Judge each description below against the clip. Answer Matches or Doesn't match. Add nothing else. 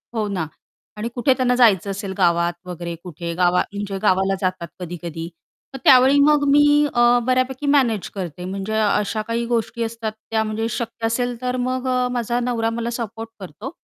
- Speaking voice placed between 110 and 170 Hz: Doesn't match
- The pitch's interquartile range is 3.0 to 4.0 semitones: Doesn't match